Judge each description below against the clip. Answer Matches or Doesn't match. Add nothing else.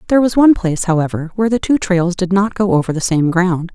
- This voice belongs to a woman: Matches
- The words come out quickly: Matches